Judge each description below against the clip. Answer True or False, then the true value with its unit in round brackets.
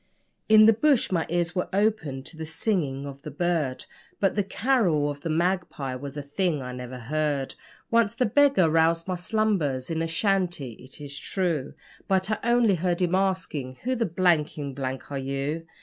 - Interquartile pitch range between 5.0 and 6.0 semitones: True (5.5 semitones)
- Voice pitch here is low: False (165 Hz)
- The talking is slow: False (185 wpm)